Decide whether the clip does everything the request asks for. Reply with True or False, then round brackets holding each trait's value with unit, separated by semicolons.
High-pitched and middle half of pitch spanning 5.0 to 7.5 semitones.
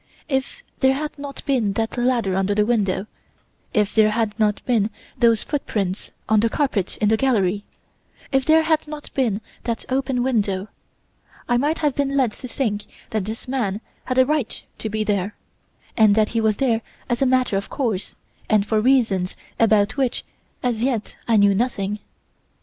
False (225 Hz; 4.1 semitones)